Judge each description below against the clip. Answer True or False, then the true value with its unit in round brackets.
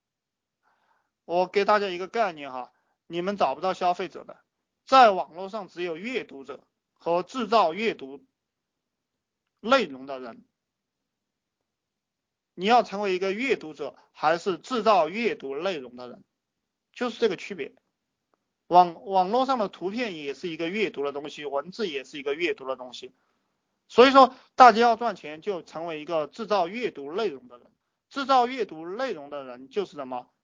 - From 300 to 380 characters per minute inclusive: False (240 characters per minute)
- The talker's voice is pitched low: False (190 Hz)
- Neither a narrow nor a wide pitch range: False (7.0 semitones)